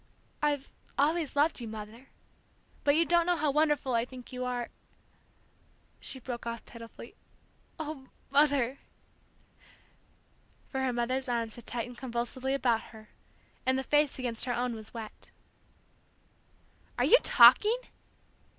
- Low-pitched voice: No, very high, 255 Hz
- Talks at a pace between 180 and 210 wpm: No, slow, 135 wpm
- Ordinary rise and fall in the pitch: Yes, average, 3.5 semitones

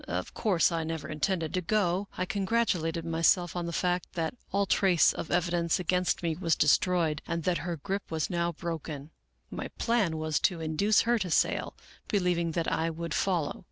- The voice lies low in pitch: No, medium, 170 Hz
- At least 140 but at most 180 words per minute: No, average, 190 wpm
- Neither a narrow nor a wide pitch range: No, narrow, 2.3 semitones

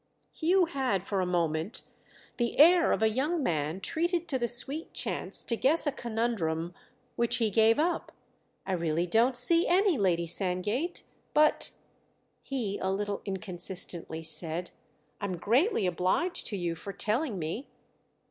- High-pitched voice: Yes, high, 220 Hz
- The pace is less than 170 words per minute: Yes, average, 145 wpm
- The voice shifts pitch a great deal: Yes, wide, 7.6 semitones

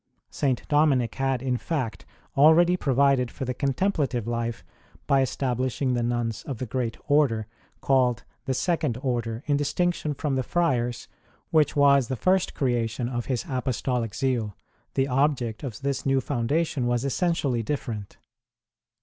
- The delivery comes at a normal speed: Yes, average, 160 wpm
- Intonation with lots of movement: No, average, 3.1 semitones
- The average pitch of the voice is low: Yes, low, 130 Hz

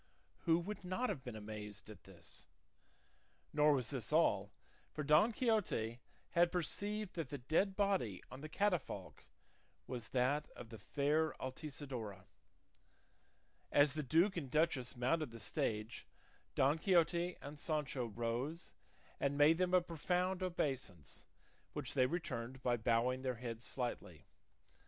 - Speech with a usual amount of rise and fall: No, wide, 6.0 semitones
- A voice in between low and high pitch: Yes, medium, 145 Hz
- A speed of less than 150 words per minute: Yes, average, 140 wpm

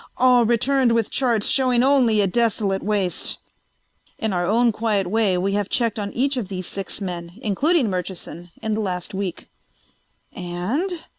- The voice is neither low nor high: No, high, 215 Hz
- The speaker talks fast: No, average, 160 wpm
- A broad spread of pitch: No, average, 4.3 semitones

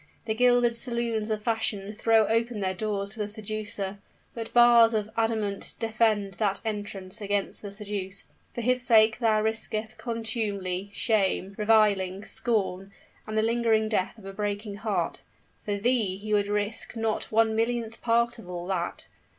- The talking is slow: No, average, 160 wpm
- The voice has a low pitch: No, high, 215 Hz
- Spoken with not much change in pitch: Yes, narrow, 2.1 semitones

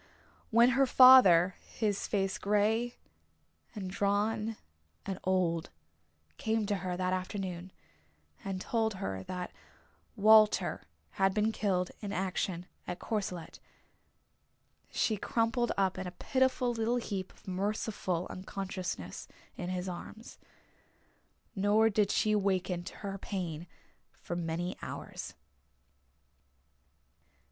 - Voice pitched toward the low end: No, high, 195 Hz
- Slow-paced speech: Yes, slow, 110 wpm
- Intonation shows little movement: No, average, 3.1 semitones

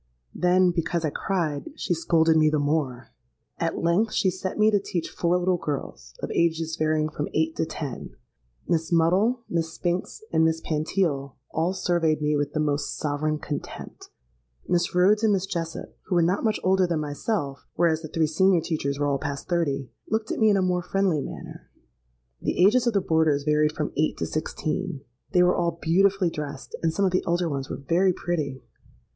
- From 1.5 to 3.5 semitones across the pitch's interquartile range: Yes, average, 3.1 semitones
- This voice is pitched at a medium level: Yes, medium, 165 Hz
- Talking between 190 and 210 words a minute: Yes, average, 195 wpm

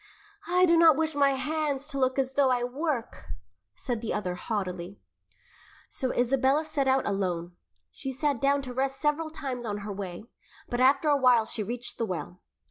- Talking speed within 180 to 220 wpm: Yes, average, 185 wpm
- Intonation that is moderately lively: Yes, average, 4.6 semitones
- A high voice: Yes, very high, 260 Hz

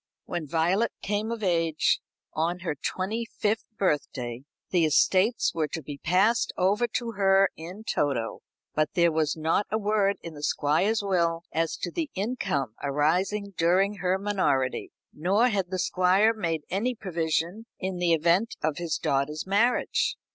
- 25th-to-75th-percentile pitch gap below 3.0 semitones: No, average, 4.4 semitones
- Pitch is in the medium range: Yes, medium, 180 Hz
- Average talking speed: Yes, average, 155 wpm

